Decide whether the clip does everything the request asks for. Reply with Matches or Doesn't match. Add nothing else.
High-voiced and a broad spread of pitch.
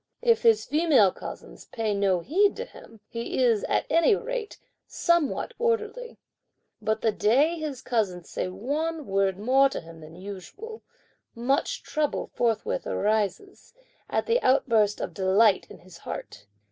Matches